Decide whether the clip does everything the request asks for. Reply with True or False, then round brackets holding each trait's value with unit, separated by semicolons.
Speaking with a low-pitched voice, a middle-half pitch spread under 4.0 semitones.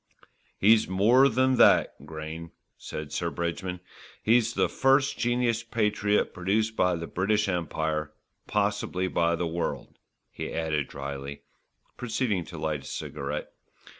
False (95 Hz; 5.6 semitones)